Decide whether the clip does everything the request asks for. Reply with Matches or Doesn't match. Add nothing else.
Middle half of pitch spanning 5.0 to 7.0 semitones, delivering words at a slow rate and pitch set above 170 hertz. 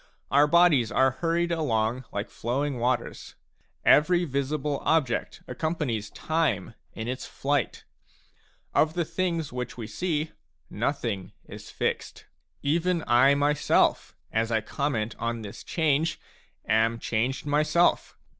Doesn't match